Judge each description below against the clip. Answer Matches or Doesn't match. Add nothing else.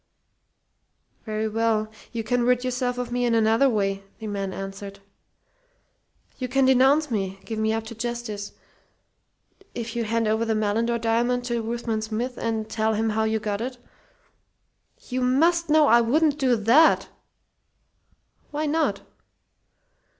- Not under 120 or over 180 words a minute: Matches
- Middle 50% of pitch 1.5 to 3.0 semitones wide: Matches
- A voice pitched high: Matches